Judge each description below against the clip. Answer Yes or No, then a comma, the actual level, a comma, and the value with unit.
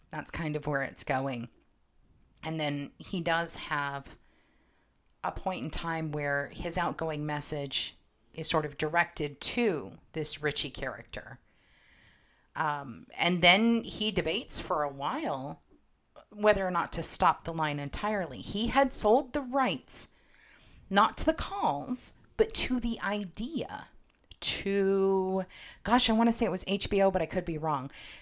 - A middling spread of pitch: No, wide, 5.9 semitones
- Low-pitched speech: No, medium, 170 Hz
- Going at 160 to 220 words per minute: No, average, 150 wpm